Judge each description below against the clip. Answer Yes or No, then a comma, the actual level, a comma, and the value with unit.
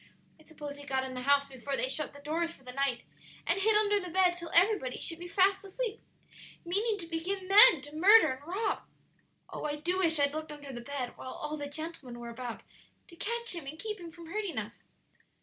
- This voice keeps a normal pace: No, fast, 225 wpm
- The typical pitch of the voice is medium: No, very high, 325 Hz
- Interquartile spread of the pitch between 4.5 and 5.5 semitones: Yes, average, 5.1 semitones